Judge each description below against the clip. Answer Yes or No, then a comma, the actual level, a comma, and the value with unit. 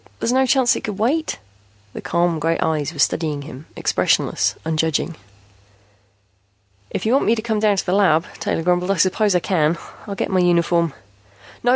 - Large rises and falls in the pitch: No, average, 4.7 semitones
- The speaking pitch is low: No, medium, 175 Hz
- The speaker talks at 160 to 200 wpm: Yes, average, 190 wpm